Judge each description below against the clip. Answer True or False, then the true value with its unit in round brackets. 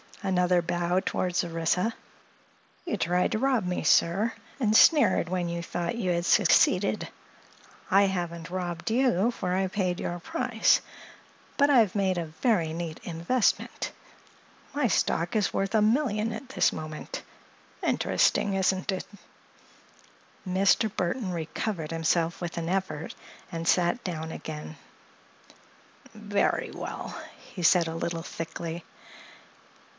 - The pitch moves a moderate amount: True (3.8 semitones)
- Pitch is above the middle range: False (180 Hz)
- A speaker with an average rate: False (130 wpm)